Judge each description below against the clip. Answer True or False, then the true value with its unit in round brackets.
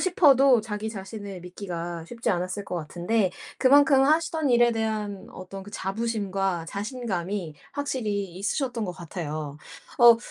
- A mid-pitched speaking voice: False (205 Hz)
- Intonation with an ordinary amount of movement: True (4.6 semitones)